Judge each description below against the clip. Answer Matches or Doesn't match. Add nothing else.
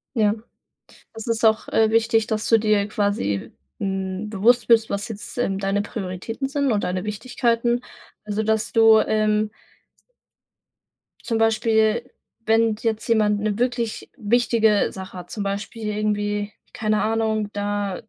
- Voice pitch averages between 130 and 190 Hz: Doesn't match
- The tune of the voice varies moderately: Doesn't match